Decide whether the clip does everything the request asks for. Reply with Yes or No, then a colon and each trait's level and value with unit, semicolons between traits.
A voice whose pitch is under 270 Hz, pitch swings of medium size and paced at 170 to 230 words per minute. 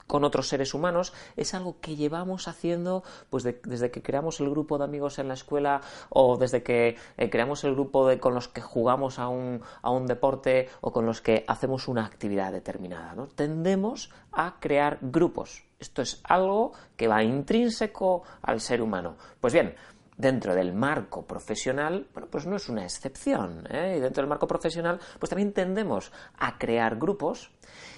No: medium, 140 Hz; wide, 5.7 semitones; average, 180 wpm